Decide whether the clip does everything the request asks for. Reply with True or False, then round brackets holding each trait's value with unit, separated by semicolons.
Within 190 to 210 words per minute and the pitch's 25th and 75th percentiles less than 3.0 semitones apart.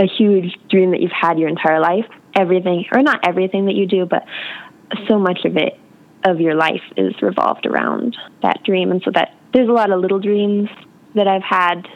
True (205 wpm; 2.5 semitones)